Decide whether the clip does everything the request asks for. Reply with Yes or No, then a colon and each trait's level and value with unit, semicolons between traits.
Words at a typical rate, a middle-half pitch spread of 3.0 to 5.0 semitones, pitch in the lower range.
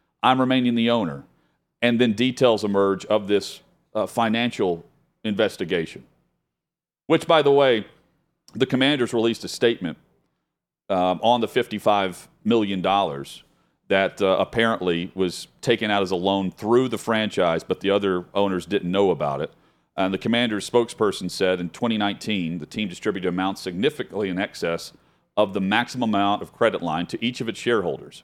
Yes: average, 155 wpm; average, 3.9 semitones; low, 105 Hz